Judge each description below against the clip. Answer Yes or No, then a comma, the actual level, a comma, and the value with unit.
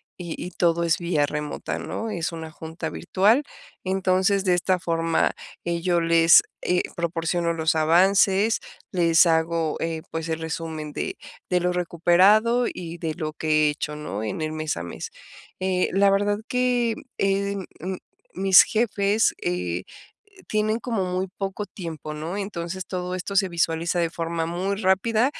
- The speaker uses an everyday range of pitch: Yes, average, 3.1 semitones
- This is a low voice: No, medium, 175 Hz